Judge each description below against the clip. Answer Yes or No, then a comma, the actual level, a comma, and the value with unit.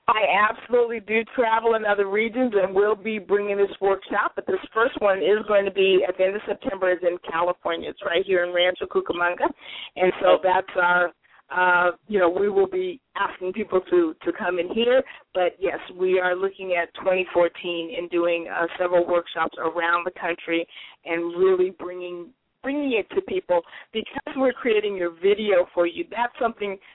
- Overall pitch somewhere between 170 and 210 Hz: Yes, high, 190 Hz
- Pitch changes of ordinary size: Yes, average, 4.0 semitones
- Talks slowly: No, average, 185 wpm